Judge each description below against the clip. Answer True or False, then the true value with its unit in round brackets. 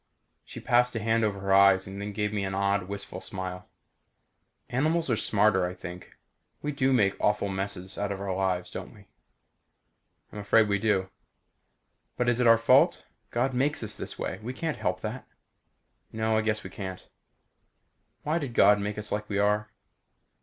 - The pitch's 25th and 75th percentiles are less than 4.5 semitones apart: True (2.8 semitones)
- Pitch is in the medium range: False (105 Hz)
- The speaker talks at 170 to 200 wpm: True (180 wpm)